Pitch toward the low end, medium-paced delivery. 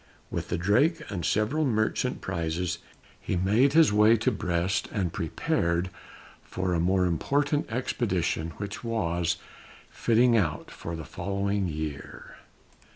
No: very low, 95 Hz; slow, 130 wpm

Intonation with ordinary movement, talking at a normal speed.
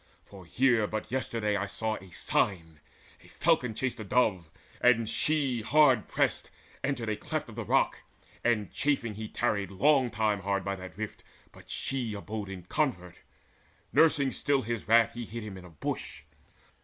Yes: average, 4.0 semitones; average, 170 wpm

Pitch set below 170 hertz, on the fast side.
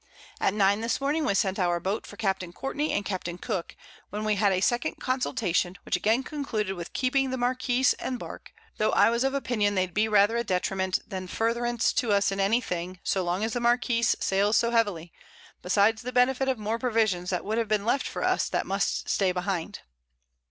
No: high, 215 Hz; fast, 210 wpm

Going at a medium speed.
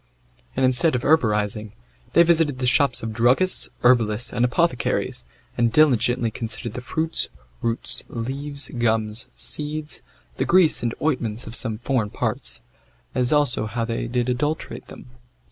Yes: average, 145 wpm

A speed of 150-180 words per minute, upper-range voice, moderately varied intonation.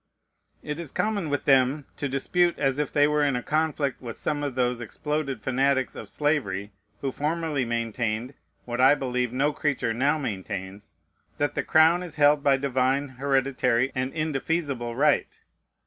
No: average, 165 wpm; low, 135 Hz; average, 3.0 semitones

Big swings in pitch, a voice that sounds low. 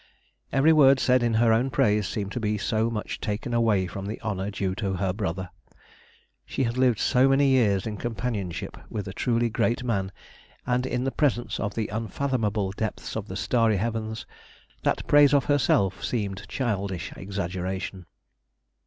No: average, 3.9 semitones; low, 110 Hz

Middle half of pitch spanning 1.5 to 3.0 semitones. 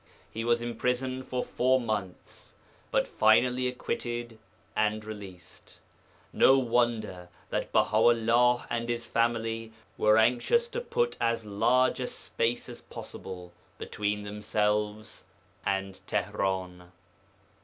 Yes: average, 2.7 semitones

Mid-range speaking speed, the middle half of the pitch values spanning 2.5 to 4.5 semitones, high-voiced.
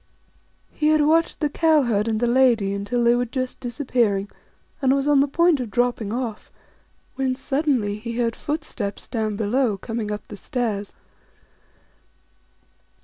Yes: average, 160 wpm; average, 4.2 semitones; high, 245 Hz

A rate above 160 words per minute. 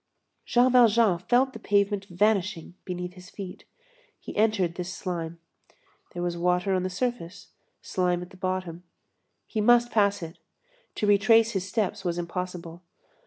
No: average, 150 wpm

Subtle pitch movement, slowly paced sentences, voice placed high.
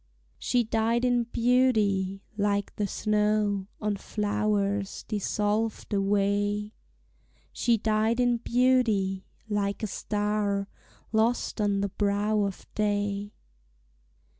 Yes: narrow, 1.6 semitones; slow, 100 wpm; high, 210 Hz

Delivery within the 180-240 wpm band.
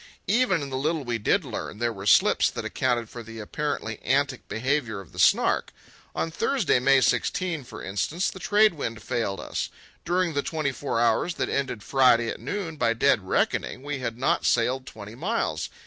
Yes: average, 190 wpm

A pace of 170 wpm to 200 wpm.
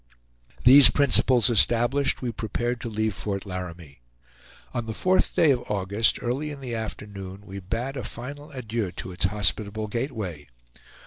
No: average, 150 wpm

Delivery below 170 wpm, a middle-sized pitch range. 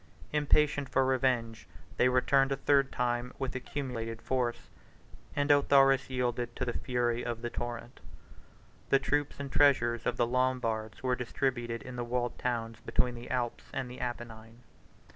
No: average, 155 wpm; narrow, 2.1 semitones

